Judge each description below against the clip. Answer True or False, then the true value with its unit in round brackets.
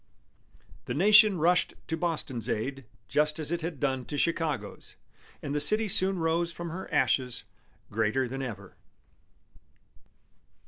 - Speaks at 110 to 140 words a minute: True (135 wpm)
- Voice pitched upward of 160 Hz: False (150 Hz)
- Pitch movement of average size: True (4.6 semitones)